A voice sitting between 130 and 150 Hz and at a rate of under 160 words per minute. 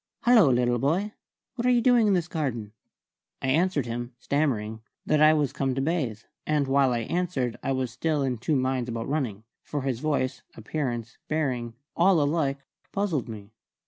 No: low, 135 Hz; average, 175 wpm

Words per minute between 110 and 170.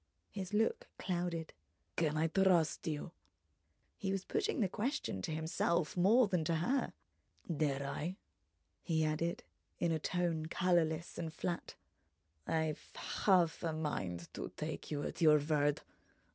Yes: average, 140 wpm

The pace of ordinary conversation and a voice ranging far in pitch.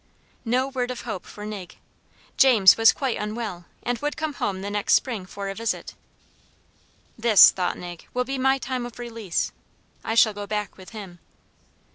No: average, 175 wpm; average, 3.9 semitones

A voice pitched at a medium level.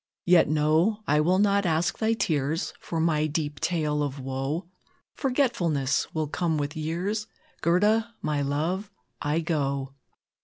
Yes: medium, 160 Hz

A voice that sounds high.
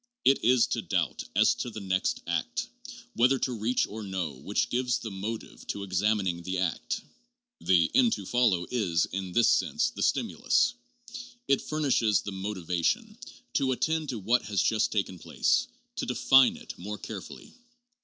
No: low, 105 Hz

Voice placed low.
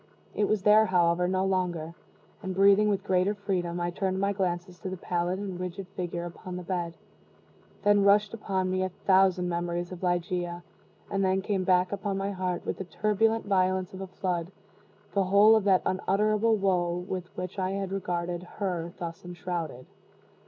No: medium, 185 Hz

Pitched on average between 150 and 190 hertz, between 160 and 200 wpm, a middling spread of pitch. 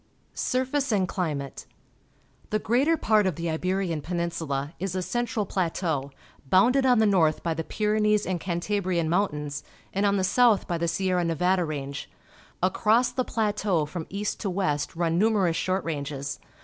Yes: medium, 185 Hz; average, 165 wpm; average, 4.4 semitones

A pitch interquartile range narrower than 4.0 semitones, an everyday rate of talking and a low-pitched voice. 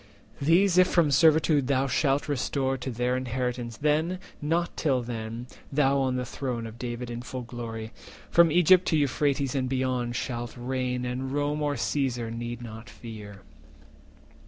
Yes: average, 3.3 semitones; average, 160 wpm; low, 130 Hz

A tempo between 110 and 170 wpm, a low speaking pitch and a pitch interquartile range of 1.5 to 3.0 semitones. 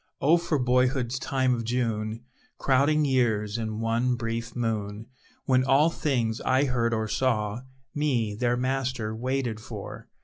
Yes: average, 140 wpm; low, 120 Hz; narrow, 2.6 semitones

